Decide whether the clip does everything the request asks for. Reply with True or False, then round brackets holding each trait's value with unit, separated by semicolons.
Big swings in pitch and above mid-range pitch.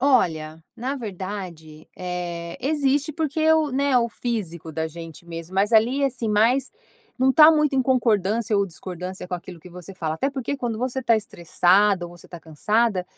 True (6.9 semitones; 210 Hz)